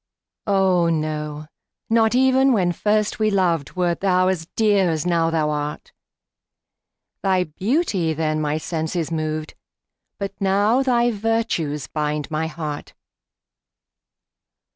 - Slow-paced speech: Yes, slow, 120 wpm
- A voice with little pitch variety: No, average, 5.0 semitones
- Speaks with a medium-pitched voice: Yes, medium, 175 Hz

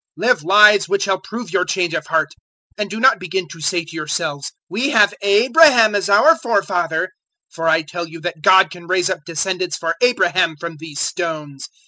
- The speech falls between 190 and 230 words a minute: Yes, average, 195 wpm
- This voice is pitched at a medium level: Yes, medium, 180 Hz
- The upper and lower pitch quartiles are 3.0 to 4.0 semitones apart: Yes, average, 3.7 semitones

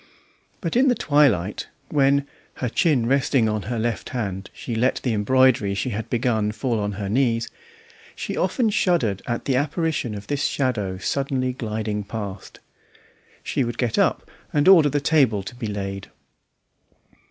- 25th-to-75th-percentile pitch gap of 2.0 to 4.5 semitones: No, average, 4.9 semitones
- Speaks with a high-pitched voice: No, low, 120 Hz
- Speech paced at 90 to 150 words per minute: No, average, 160 wpm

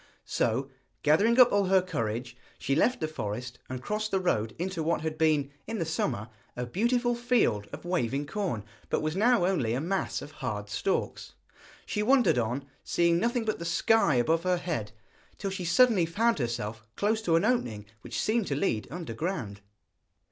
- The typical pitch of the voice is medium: Yes, medium, 170 Hz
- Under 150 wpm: No, average, 180 wpm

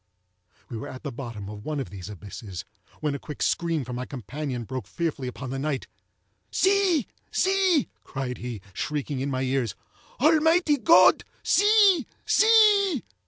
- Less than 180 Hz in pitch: Yes, medium, 140 Hz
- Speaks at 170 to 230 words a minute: No, average, 155 wpm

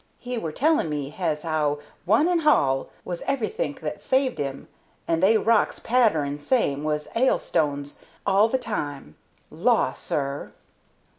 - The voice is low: No, medium, 170 Hz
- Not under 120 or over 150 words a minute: Yes, slow, 135 wpm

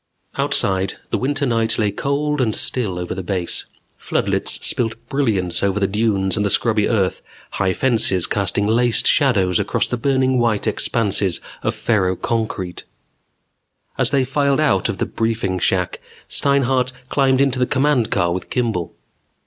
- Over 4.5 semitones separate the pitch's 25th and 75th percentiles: Yes, average, 5.3 semitones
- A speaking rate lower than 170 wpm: Yes, average, 150 wpm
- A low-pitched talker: Yes, low, 115 Hz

